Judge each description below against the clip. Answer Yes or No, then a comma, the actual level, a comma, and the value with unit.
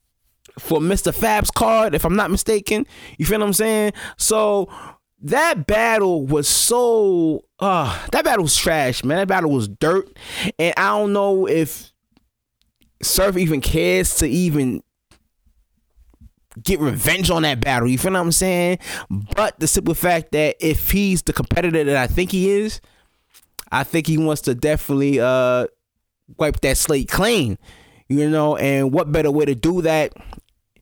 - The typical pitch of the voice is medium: Yes, medium, 165 Hz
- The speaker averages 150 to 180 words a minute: Yes, average, 160 wpm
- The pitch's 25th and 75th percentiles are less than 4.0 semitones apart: No, average, 5.2 semitones